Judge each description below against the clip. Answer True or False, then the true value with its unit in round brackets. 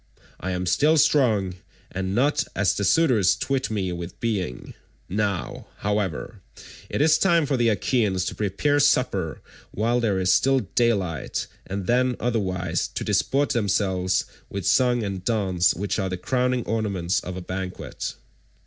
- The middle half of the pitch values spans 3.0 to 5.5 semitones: True (5.0 semitones)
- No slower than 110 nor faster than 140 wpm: False (150 wpm)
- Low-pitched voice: True (100 Hz)